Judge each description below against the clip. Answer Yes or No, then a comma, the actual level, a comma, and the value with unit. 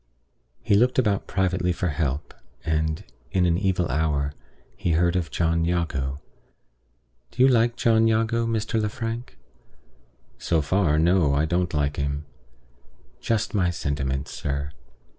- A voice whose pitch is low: Yes, very low, 85 Hz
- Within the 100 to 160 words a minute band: Yes, slow, 135 wpm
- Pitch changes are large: Yes, wide, 5.9 semitones